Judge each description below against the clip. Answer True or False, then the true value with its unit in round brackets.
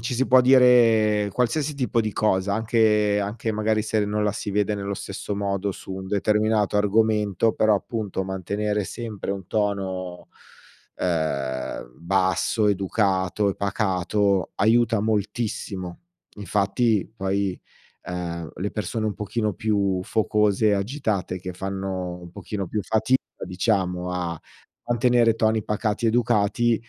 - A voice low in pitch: True (105 Hz)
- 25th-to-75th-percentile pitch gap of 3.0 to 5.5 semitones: False (2.5 semitones)